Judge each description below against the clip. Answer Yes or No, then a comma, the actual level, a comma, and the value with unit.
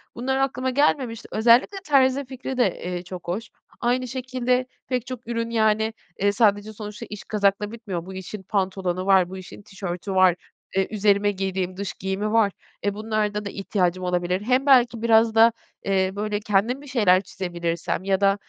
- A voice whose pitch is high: Yes, high, 210 Hz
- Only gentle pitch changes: No, average, 3.7 semitones